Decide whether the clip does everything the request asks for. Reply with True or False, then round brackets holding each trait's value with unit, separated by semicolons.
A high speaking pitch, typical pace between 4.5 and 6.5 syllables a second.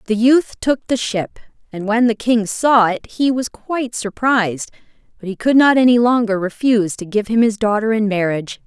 True (225 Hz; 5.1 syllables/s)